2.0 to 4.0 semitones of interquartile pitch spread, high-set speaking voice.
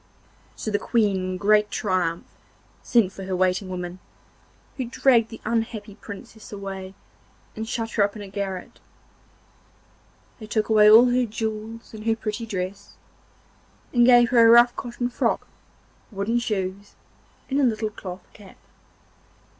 Yes: average, 3.0 semitones; high, 215 Hz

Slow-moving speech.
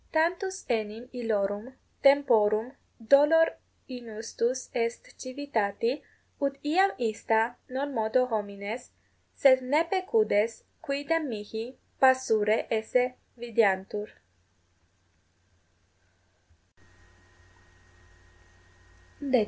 Yes: slow, 70 wpm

